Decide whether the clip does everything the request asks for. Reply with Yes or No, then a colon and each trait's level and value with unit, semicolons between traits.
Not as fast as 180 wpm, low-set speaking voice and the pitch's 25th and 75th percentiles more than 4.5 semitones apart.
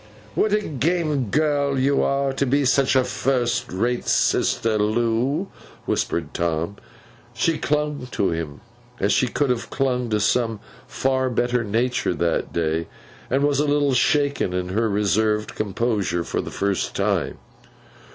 Yes: average, 150 wpm; low, 125 Hz; average, 5.1 semitones